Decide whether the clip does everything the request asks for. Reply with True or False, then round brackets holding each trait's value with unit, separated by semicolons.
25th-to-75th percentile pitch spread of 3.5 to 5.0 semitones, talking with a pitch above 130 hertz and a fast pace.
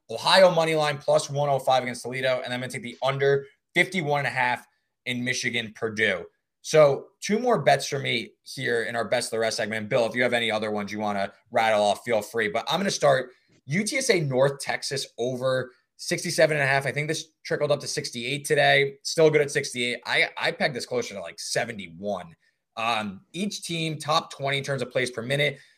True (4.0 semitones; 140 Hz; 210 wpm)